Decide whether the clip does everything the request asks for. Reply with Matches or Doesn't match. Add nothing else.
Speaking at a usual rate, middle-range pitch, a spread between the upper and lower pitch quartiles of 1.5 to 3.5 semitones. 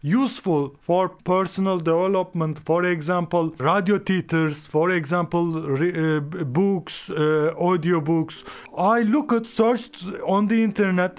Matches